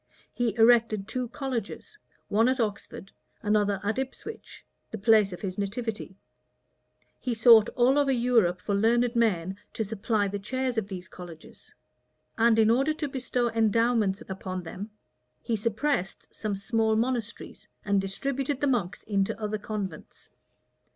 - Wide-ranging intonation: No, average, 3.4 semitones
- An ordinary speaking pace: Yes, average, 145 wpm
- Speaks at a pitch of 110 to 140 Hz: No, high, 220 Hz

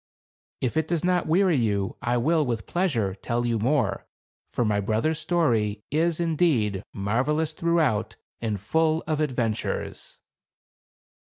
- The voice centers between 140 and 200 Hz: No, low, 130 Hz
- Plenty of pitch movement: Yes, wide, 6.9 semitones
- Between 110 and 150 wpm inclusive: Yes, average, 140 wpm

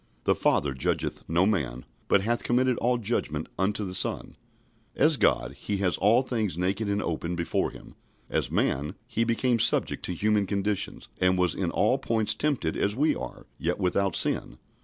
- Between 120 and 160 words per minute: No, average, 180 wpm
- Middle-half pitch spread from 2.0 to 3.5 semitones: No, average, 4.4 semitones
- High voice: No, low, 100 Hz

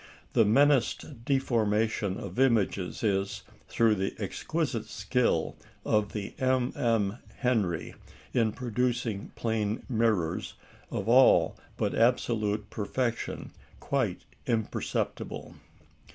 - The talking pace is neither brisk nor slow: No, slow, 95 wpm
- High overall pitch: No, low, 115 Hz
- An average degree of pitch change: Yes, average, 3.1 semitones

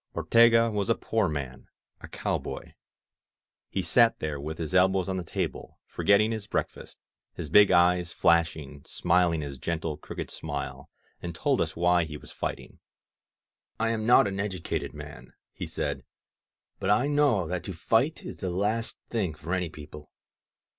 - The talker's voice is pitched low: Yes, very low, 90 Hz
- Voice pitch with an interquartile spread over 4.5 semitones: Yes, average, 5.0 semitones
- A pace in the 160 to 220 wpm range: Yes, average, 165 wpm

